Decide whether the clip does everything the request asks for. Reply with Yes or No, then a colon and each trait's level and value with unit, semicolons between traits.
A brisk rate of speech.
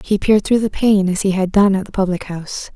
Yes: fast, 285 wpm